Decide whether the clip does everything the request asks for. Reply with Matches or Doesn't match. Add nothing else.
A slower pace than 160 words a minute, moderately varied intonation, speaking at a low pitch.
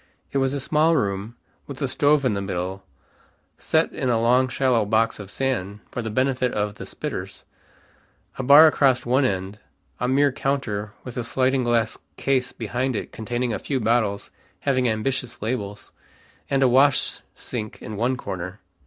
Doesn't match